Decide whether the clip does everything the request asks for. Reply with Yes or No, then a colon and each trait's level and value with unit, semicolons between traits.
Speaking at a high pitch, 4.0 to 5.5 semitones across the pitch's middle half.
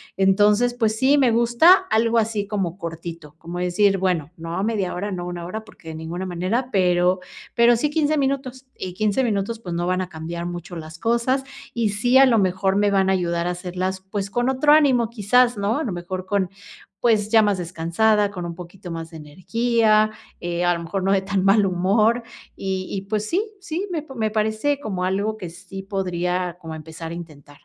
Yes: high, 195 Hz; average, 4.4 semitones